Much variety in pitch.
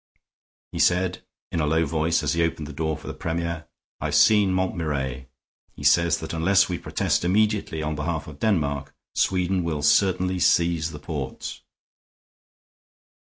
No: average, 3.2 semitones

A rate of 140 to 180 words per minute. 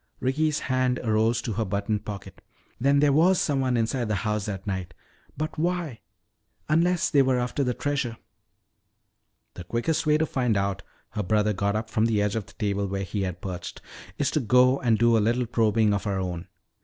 No: average, 195 wpm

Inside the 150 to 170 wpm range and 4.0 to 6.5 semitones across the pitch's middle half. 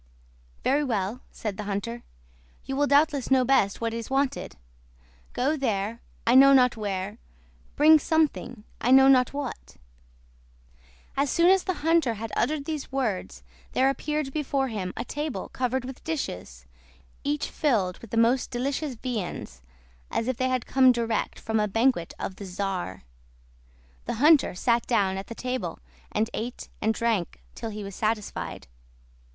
Yes: average, 160 wpm; average, 4.5 semitones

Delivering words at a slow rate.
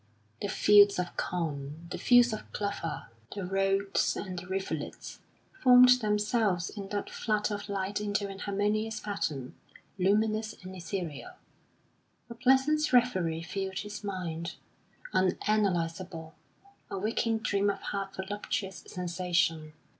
Yes: slow, 125 wpm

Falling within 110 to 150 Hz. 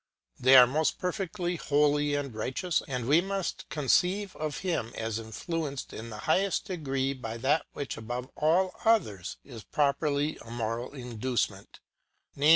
Yes: medium, 140 Hz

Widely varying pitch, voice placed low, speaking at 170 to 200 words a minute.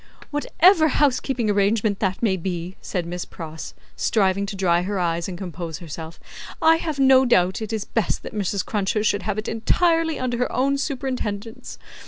No: wide, 6.0 semitones; high, 210 Hz; average, 175 wpm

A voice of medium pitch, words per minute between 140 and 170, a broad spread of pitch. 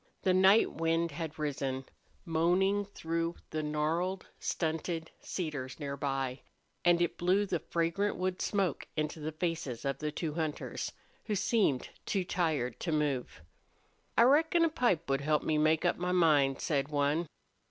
No: medium, 165 Hz; average, 155 wpm; average, 3.5 semitones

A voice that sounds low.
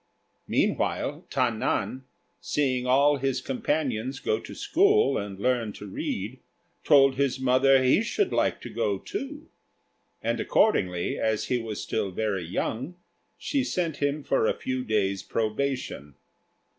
Yes: low, 130 Hz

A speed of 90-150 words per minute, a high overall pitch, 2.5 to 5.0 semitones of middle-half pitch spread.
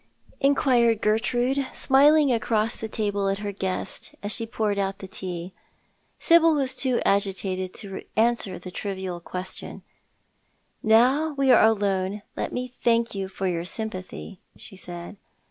Yes: average, 145 wpm; high, 210 Hz; average, 4.2 semitones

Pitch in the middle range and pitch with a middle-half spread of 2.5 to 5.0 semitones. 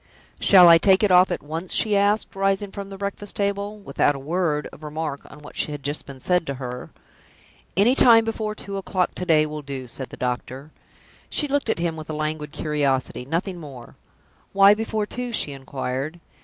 No: medium, 165 Hz; wide, 5.6 semitones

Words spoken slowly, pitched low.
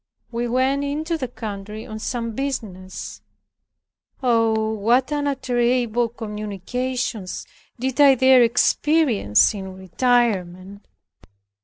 No: slow, 95 wpm; high, 235 Hz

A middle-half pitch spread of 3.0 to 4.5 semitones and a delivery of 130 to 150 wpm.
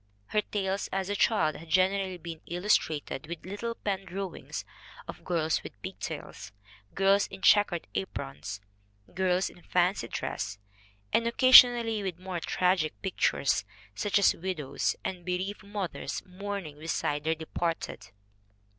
Yes: average, 3.5 semitones; slow, 135 wpm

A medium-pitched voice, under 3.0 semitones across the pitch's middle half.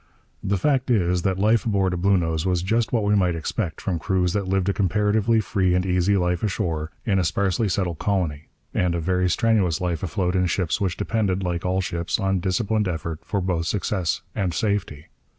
No: very low, 95 Hz; narrow, 2.5 semitones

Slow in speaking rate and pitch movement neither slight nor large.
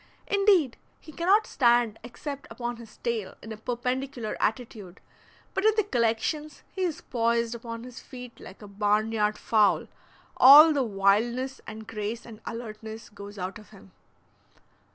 No: average, 155 wpm; average, 3.4 semitones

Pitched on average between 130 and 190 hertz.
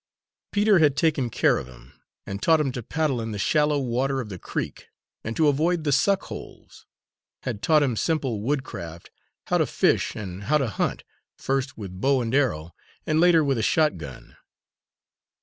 Yes: low, 135 Hz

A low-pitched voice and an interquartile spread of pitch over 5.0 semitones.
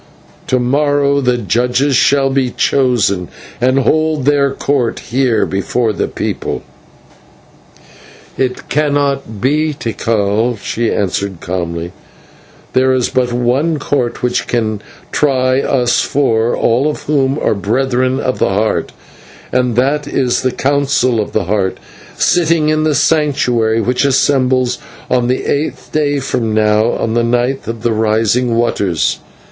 No: low, 125 Hz; average, 3.5 semitones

